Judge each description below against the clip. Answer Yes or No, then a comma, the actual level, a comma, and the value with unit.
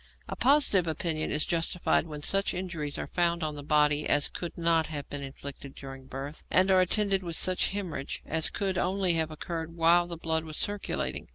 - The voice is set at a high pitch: No, medium, 165 Hz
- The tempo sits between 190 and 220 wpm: Yes, average, 195 wpm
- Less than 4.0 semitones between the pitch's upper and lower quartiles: Yes, average, 3.4 semitones